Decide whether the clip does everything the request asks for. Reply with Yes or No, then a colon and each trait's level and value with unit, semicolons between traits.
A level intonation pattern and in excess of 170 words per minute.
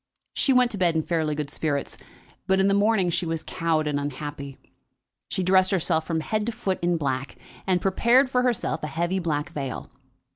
No: average, 4.1 semitones; average, 195 wpm